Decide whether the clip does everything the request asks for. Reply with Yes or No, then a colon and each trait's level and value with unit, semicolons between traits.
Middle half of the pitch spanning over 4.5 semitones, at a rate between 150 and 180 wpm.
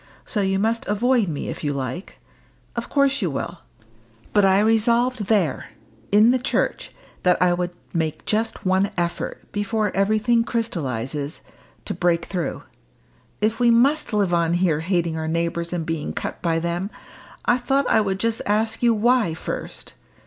Yes: average, 5.1 semitones; average, 165 wpm